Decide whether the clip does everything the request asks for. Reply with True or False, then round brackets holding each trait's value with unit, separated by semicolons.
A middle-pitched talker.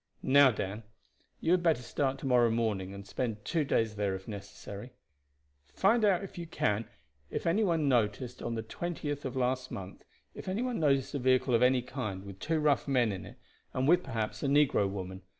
False (125 Hz)